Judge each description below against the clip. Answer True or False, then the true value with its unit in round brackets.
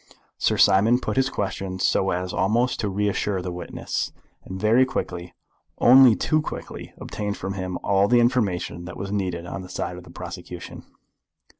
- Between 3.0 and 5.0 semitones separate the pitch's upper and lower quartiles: True (3.8 semitones)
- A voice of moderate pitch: False (95 Hz)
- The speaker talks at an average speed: True (170 wpm)